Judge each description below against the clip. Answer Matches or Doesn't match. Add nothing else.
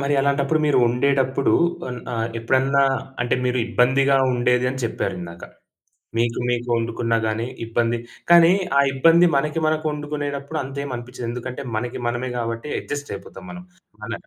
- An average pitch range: Matches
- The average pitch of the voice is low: Matches